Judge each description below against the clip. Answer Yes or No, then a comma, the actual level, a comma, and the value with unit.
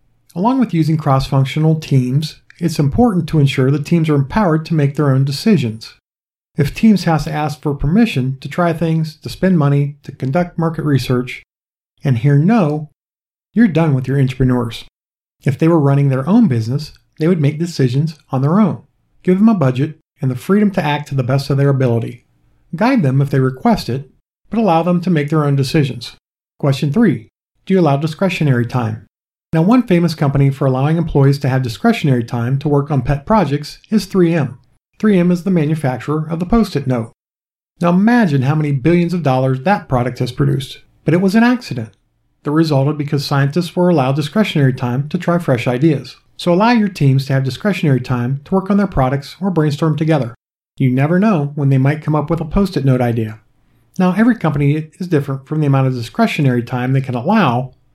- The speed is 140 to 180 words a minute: No, average, 200 wpm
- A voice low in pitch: No, medium, 145 Hz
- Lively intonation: No, average, 4.5 semitones